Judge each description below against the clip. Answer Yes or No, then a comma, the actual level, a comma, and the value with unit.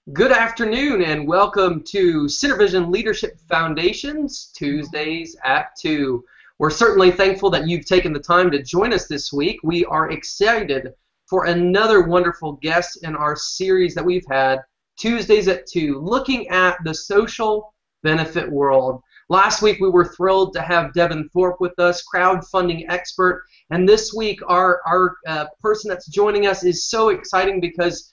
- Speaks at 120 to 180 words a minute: Yes, average, 160 wpm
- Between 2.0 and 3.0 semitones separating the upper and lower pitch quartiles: No, average, 3.7 semitones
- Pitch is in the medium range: Yes, medium, 180 Hz